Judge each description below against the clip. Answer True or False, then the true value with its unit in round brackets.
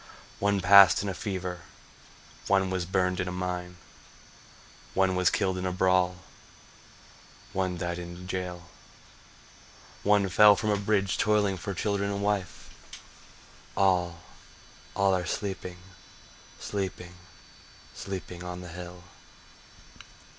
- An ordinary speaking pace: False (120 wpm)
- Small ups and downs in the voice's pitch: True (1.8 semitones)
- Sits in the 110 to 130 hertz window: False (95 Hz)